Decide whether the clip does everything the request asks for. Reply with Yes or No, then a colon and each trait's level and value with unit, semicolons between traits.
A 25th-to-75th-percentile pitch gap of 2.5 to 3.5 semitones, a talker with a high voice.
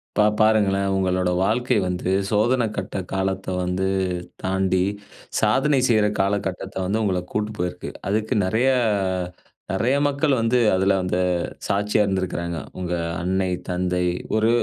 No: average, 2.8 semitones; very low, 95 Hz